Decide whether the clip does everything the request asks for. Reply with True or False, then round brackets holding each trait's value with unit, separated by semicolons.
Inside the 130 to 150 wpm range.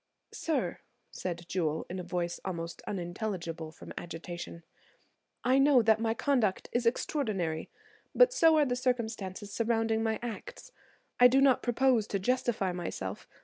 True (145 wpm)